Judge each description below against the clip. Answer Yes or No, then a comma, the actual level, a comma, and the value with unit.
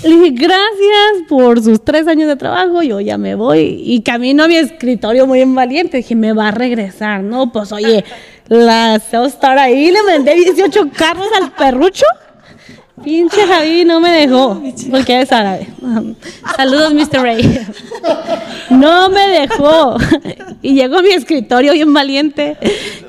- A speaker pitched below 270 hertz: No, very high, 275 Hz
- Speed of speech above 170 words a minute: No, average, 155 wpm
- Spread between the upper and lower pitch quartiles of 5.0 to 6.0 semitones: Yes, wide, 5.6 semitones